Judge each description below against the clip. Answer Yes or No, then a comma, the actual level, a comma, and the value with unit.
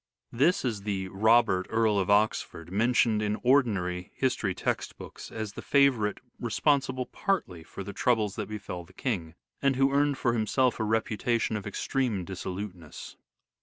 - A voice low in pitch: Yes, low, 110 Hz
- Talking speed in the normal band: Yes, average, 155 wpm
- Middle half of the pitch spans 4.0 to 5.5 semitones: Yes, average, 4.4 semitones